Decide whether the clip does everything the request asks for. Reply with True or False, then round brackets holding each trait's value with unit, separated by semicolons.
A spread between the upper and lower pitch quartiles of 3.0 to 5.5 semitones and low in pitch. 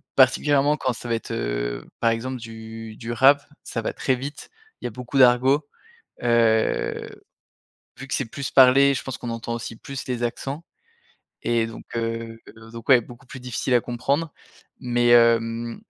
False (2.6 semitones; 120 Hz)